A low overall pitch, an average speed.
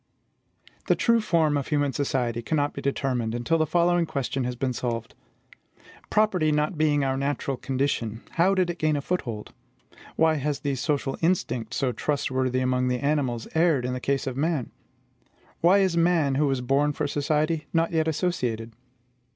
No: medium, 145 Hz; average, 170 wpm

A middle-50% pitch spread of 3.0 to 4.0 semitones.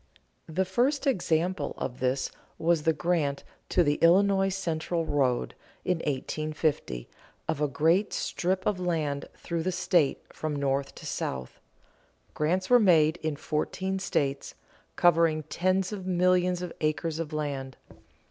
Yes: average, 3.6 semitones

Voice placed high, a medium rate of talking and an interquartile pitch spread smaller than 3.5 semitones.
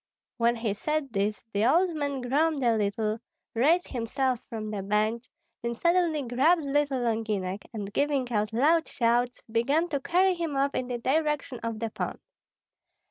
No: very high, 250 Hz; average, 170 wpm; average, 4.8 semitones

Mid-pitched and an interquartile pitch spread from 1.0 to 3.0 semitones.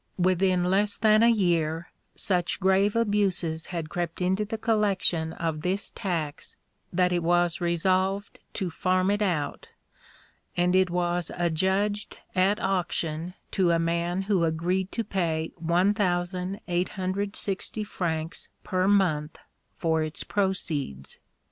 Yes: medium, 180 Hz; narrow, 2.5 semitones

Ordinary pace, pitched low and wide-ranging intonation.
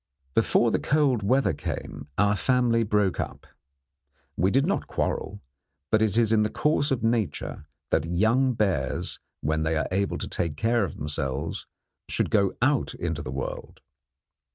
Yes: average, 160 wpm; low, 105 Hz; wide, 6.4 semitones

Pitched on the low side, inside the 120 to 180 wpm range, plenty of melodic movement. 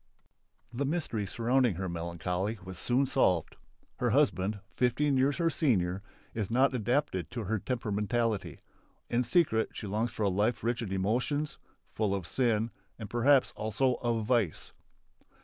No: low, 115 Hz; average, 150 wpm; average, 4.4 semitones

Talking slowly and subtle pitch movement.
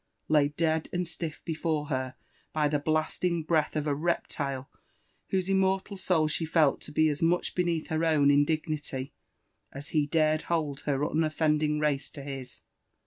No: average, 155 wpm; narrow, 2.2 semitones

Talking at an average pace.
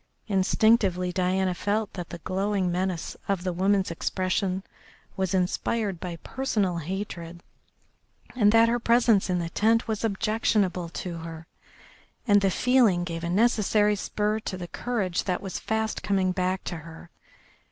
Yes: average, 150 wpm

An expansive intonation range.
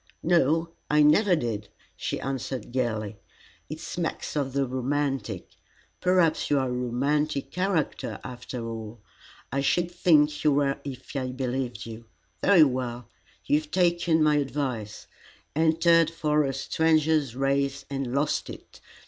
No: average, 3.6 semitones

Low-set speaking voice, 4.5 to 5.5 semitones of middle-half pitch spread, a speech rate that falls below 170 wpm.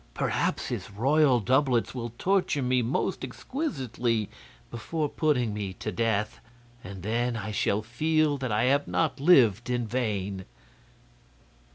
Yes: low, 120 Hz; average, 4.8 semitones; slow, 135 wpm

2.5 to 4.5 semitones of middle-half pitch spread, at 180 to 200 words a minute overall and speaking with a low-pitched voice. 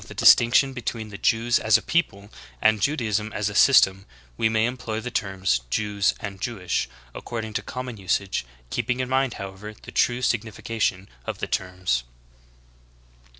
No: average, 3.6 semitones; average, 155 wpm; low, 110 Hz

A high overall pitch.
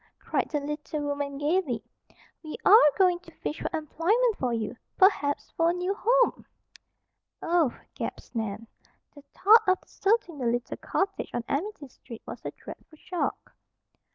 Yes: very high, 310 Hz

